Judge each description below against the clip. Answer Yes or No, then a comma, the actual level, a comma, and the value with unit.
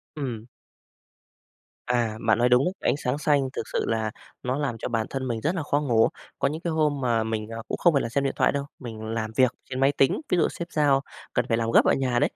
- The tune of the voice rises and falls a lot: No, average, 3.9 semitones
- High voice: No, low, 125 Hz